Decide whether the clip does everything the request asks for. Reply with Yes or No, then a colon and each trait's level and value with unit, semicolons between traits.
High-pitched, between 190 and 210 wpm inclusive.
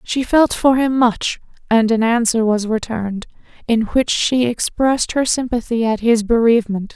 No: high, 230 Hz; average, 165 wpm